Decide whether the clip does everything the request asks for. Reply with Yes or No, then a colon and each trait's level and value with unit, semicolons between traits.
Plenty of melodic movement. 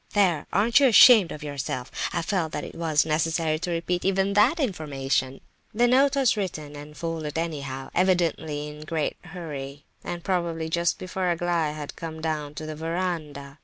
No: average, 3.4 semitones